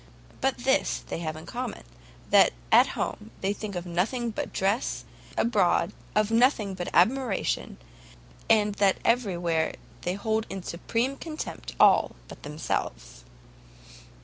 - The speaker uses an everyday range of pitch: Yes, average, 4.7 semitones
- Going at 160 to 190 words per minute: No, slow, 135 wpm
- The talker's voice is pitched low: No, high, 200 Hz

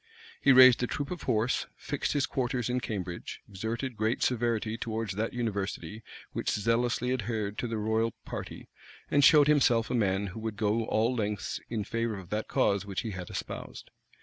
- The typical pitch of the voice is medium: No, low, 115 Hz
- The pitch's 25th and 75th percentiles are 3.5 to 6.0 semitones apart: No, average, 2.7 semitones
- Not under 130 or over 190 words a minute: Yes, average, 180 wpm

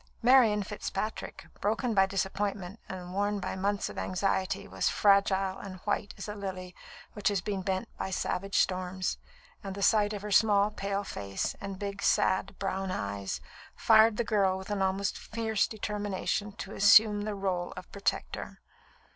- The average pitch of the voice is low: No, high, 200 Hz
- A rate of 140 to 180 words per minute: Yes, average, 165 wpm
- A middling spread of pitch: No, narrow, 1.6 semitones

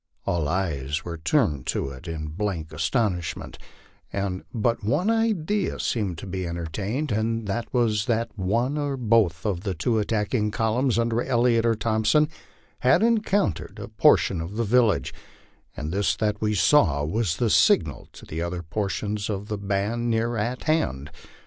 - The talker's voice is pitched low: Yes, low, 105 Hz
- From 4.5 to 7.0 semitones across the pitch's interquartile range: Yes, average, 5.1 semitones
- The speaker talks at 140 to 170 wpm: Yes, average, 160 wpm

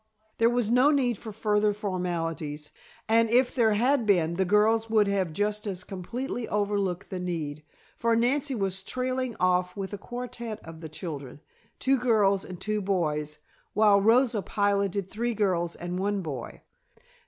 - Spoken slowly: No, average, 160 wpm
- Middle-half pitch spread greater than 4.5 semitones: No, average, 4.1 semitones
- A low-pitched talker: No, high, 205 Hz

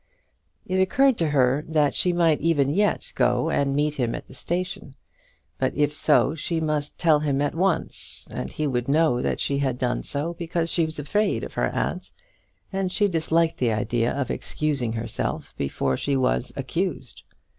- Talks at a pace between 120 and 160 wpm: No, average, 180 wpm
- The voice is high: No, medium, 150 Hz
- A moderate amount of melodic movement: Yes, average, 4.0 semitones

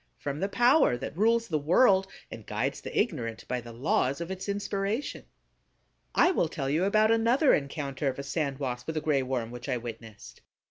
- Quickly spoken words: No, average, 195 wpm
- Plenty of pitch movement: Yes, wide, 7.9 semitones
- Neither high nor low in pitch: Yes, medium, 150 Hz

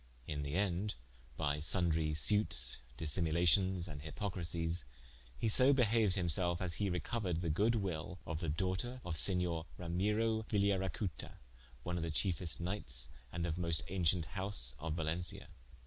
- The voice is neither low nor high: No, very low, 90 Hz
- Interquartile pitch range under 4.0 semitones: Yes, average, 3.5 semitones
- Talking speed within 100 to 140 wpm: No, average, 150 wpm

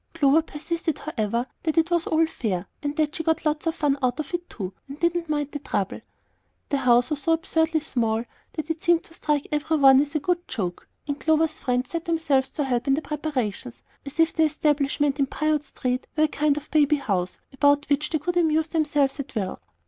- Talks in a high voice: Yes, very high, 295 Hz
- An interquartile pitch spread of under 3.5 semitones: Yes, average, 2.9 semitones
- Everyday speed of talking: No, fast, 215 wpm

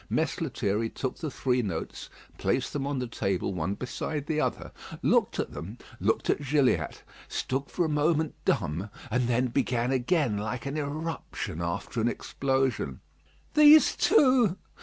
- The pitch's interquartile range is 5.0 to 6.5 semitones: Yes, average, 5.3 semitones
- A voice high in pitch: No, low, 130 Hz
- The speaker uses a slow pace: No, average, 155 wpm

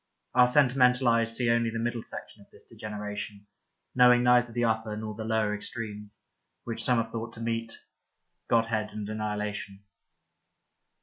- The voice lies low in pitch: Yes, low, 115 Hz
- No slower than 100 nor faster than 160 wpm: Yes, average, 150 wpm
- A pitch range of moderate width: No, narrow, 2.0 semitones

